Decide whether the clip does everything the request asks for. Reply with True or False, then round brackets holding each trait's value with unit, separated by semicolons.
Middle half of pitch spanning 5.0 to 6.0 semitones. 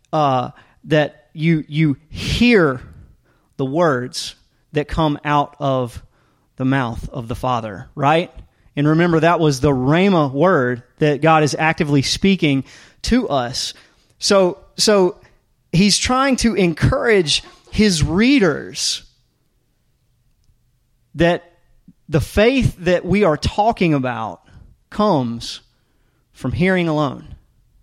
True (5.4 semitones)